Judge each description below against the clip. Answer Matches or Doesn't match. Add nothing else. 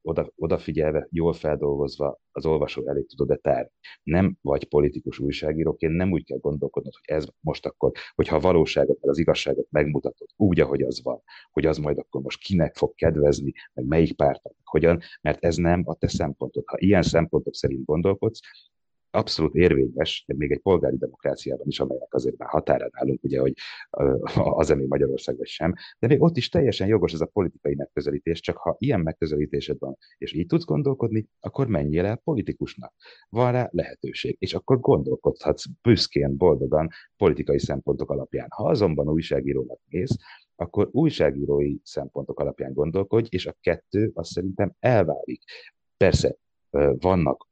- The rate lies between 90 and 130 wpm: Doesn't match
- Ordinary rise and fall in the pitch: Doesn't match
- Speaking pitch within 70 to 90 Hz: Matches